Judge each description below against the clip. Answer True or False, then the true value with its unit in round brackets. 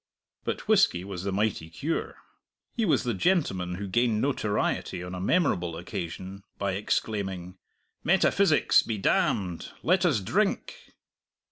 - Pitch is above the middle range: False (100 Hz)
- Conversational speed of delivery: False (130 wpm)